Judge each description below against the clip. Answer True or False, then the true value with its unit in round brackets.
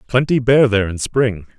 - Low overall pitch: True (115 Hz)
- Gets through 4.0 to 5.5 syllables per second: True (5.2 syllables/s)